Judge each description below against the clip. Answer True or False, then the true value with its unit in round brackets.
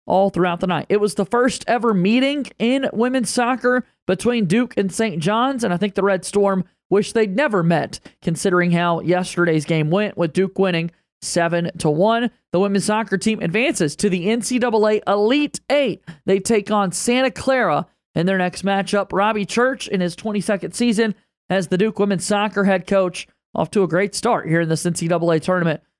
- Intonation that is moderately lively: True (4.0 semitones)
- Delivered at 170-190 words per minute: True (185 wpm)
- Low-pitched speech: False (200 Hz)